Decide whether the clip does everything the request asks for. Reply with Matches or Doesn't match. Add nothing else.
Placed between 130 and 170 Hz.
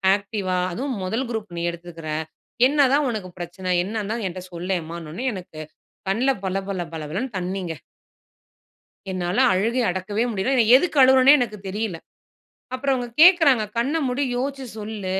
Doesn't match